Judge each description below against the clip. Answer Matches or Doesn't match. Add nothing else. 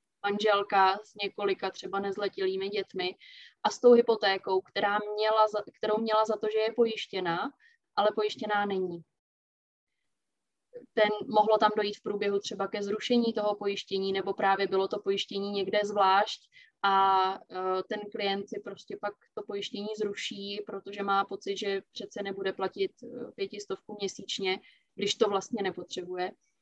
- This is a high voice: Matches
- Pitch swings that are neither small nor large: Doesn't match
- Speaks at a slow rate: Doesn't match